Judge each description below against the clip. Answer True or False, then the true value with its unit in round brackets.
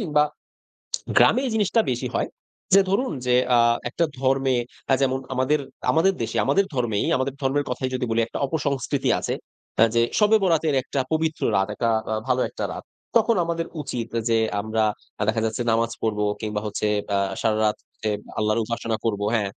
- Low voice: True (130 Hz)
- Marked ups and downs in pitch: True (5.8 semitones)